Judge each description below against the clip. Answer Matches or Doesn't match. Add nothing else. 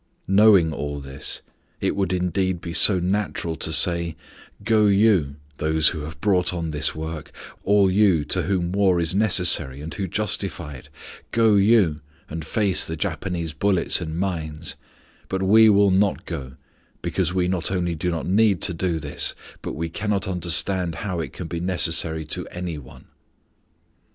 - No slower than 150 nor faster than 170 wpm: Matches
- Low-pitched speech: Matches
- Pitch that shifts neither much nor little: Matches